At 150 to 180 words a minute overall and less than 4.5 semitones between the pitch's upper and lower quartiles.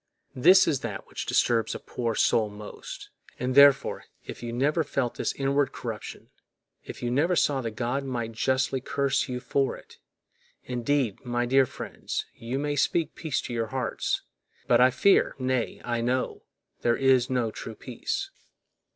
Yes: average, 165 wpm; average, 2.7 semitones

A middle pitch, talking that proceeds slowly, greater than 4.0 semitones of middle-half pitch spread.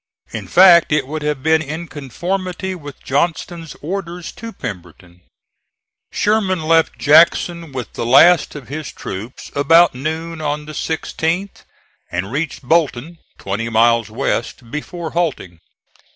Yes: medium, 155 Hz; slow, 130 wpm; average, 4.7 semitones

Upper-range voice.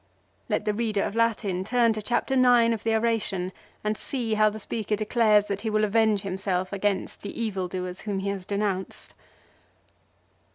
Yes: high, 210 Hz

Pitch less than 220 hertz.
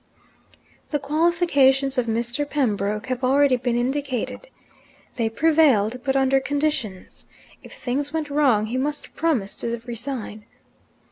No: very high, 265 Hz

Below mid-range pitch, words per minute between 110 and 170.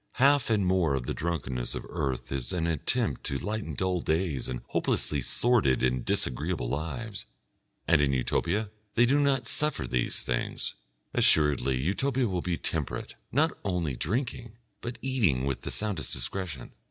Yes: very low, 85 Hz; average, 155 wpm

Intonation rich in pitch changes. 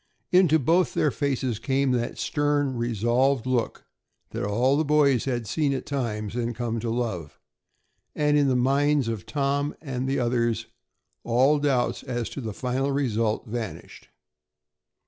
No: average, 3.3 semitones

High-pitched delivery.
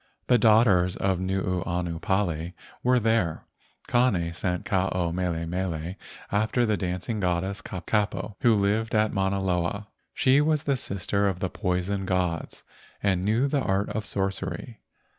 No: very low, 95 Hz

